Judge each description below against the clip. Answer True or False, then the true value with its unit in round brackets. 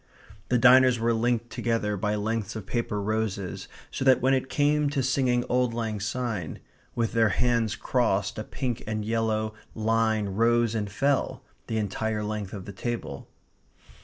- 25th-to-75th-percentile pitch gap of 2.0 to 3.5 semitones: True (2.6 semitones)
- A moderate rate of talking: True (160 wpm)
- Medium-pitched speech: False (115 Hz)